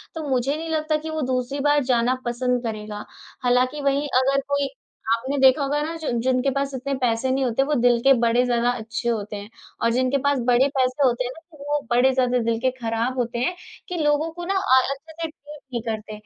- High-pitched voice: Yes, very high, 260 Hz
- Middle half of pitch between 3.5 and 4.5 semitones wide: No, average, 3.0 semitones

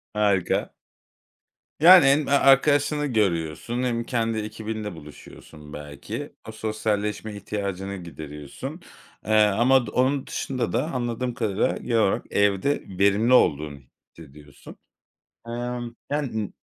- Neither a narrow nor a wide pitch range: Yes, average, 4.5 semitones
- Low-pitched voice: Yes, low, 110 Hz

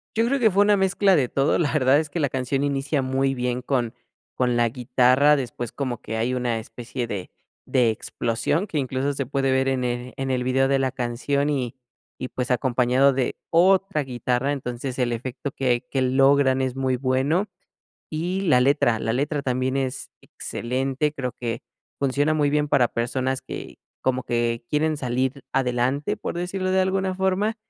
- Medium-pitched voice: No, low, 130 Hz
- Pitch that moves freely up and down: No, average, 2.7 semitones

